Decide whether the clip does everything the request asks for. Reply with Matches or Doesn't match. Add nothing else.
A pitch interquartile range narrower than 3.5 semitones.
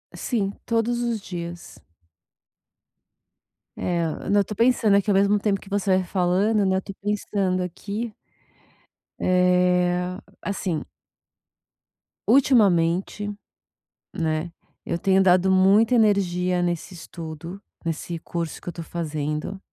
Matches